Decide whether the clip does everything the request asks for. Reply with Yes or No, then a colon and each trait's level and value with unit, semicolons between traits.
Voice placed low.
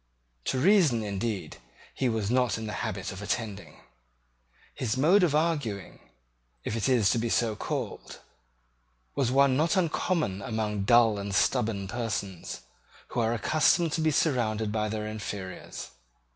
Yes: low, 115 Hz